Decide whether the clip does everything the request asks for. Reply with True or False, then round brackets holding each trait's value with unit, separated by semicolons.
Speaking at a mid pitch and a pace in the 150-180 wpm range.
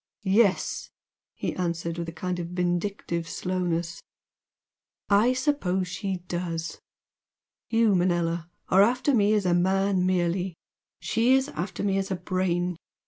False (180 Hz; 135 wpm)